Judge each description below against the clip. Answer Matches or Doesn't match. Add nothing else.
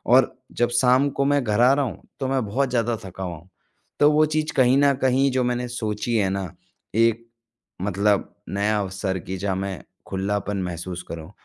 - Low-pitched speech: Matches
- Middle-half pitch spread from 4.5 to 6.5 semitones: Matches